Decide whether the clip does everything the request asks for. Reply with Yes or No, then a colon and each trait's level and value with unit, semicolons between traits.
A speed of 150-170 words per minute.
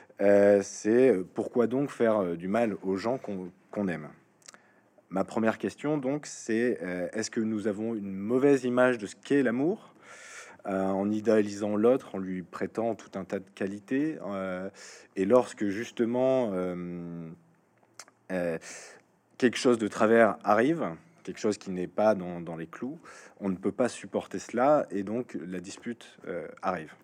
Yes: average, 160 wpm